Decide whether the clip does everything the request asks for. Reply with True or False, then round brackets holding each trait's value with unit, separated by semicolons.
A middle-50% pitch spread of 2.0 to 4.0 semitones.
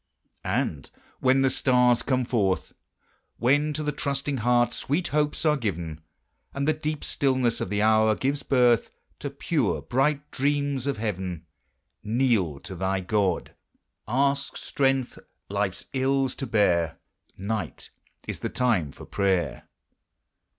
False (5.4 semitones)